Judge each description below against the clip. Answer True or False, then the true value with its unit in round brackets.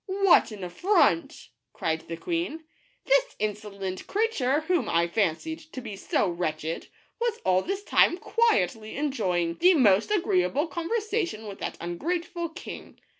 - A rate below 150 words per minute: True (140 wpm)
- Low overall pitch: False (280 Hz)